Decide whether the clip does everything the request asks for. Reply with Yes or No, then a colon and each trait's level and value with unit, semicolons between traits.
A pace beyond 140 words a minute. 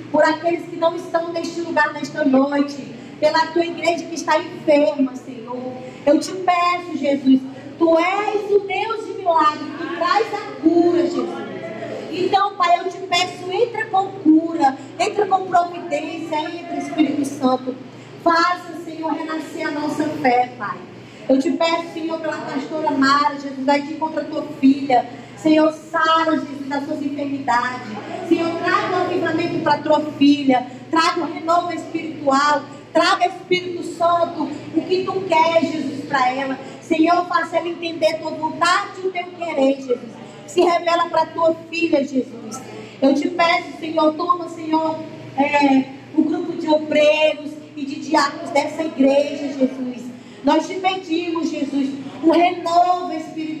Yes: average, 155 wpm